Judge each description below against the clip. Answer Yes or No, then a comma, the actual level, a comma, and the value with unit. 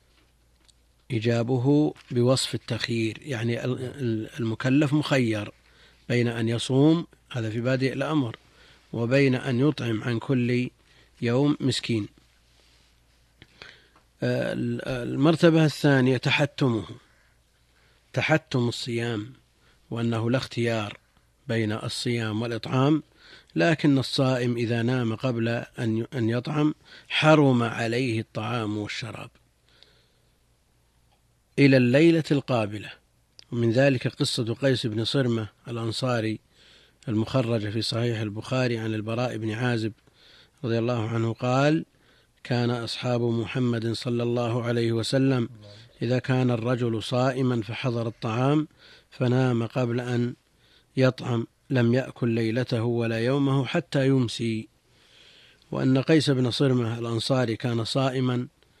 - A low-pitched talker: Yes, low, 120 Hz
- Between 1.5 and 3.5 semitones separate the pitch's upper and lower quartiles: Yes, narrow, 2.6 semitones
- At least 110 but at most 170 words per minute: No, average, 95 wpm